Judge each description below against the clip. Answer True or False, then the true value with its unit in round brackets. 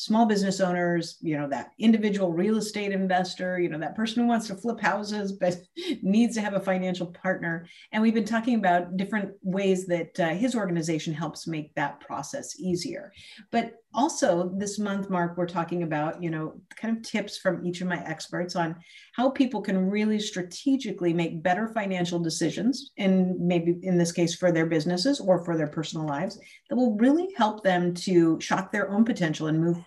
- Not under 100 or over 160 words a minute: False (195 wpm)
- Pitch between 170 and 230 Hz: True (185 Hz)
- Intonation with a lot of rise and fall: False (3.8 semitones)